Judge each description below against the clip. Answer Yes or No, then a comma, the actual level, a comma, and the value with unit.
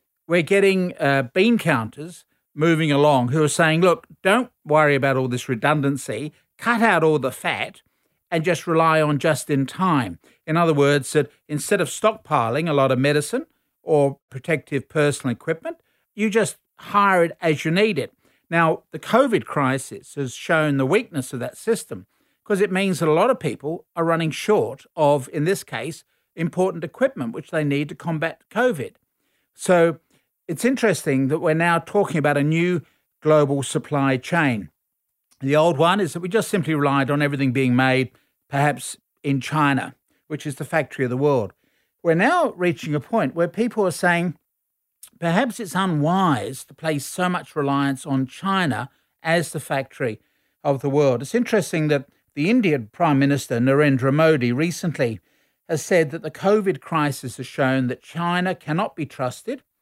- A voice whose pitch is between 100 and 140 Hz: No, medium, 155 Hz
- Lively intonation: No, average, 4.1 semitones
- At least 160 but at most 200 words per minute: Yes, average, 170 wpm